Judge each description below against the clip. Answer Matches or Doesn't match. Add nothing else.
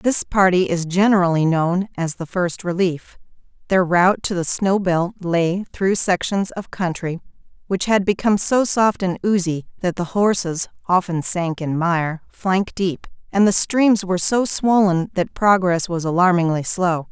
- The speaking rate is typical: Matches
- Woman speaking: Matches